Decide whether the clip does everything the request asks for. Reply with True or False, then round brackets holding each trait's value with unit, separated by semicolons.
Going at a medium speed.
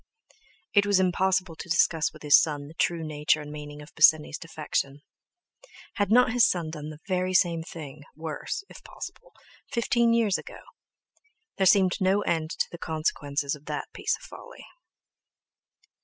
True (160 wpm)